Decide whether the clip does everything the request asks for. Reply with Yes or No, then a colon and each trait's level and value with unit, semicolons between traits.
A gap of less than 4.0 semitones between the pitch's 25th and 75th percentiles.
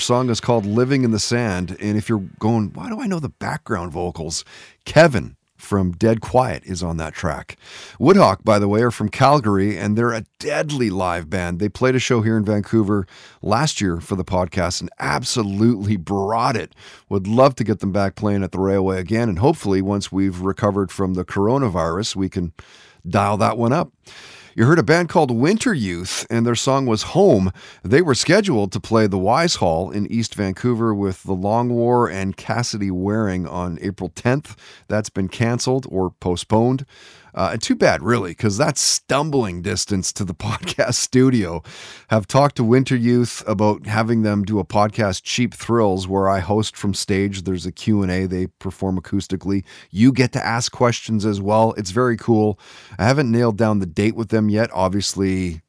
Yes: average, 3.5 semitones